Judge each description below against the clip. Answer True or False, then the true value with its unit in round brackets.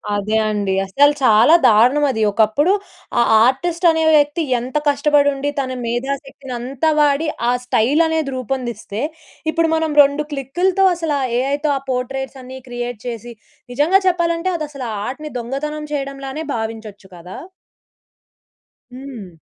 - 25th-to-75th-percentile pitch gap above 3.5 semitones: True (3.9 semitones)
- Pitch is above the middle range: True (275 Hz)